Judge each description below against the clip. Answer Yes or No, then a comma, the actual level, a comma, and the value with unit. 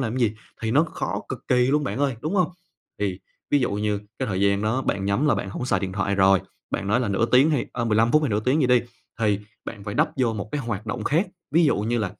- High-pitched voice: No, low, 115 Hz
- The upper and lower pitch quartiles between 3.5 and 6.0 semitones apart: Yes, average, 4.5 semitones